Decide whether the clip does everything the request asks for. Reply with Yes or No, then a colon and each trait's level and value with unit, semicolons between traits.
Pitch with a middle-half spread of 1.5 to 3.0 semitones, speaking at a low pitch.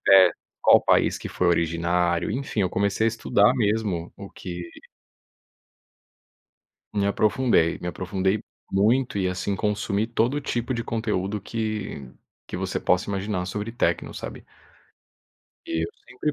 No: average, 3.5 semitones; low, 100 Hz